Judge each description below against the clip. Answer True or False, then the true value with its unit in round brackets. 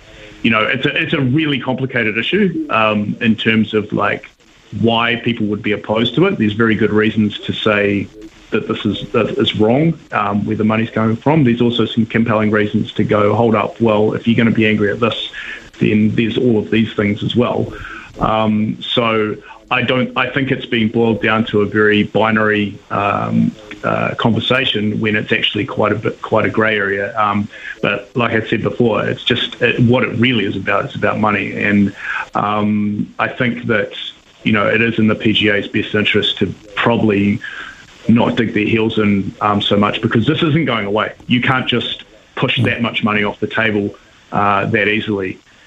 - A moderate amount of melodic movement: False (2.0 semitones)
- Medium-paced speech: True (195 wpm)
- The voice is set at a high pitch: False (110 Hz)